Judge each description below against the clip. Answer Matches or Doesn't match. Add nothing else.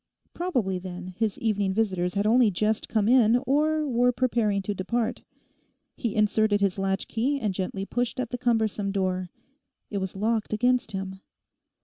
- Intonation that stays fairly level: Doesn't match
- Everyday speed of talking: Matches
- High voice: Matches